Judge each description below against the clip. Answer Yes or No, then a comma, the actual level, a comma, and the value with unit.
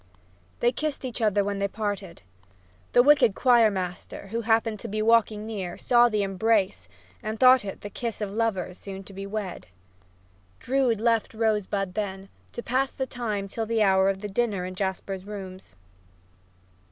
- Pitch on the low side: No, high, 210 Hz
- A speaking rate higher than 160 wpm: Yes, average, 170 wpm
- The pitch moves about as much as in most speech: Yes, average, 3.0 semitones